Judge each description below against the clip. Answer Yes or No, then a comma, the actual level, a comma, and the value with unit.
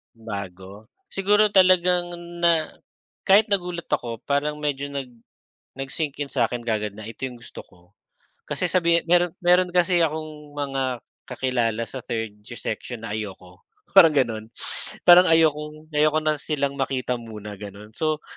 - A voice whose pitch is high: No, medium, 140 Hz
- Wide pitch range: Yes, wide, 6.6 semitones